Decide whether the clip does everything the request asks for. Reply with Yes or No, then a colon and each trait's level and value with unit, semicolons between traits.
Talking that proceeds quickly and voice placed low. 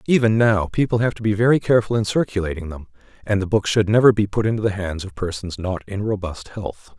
Yes: fast, 230 wpm; low, 100 Hz